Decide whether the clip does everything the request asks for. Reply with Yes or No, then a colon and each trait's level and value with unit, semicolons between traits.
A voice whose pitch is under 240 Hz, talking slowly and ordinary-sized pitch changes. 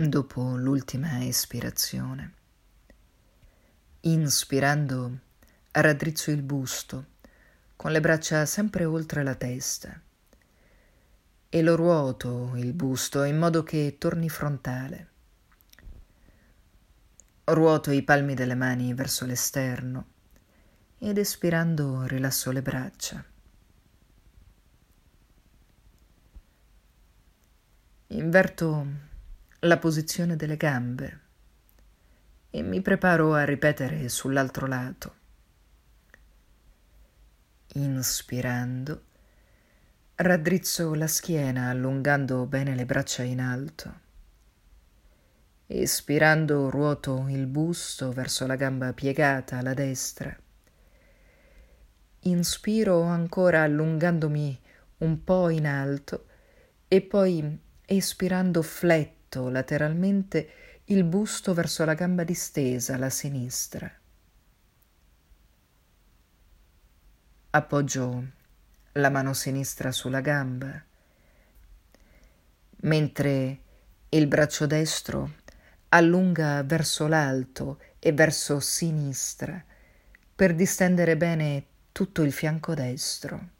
Yes: medium, 140 Hz; slow, 80 wpm; average, 4.3 semitones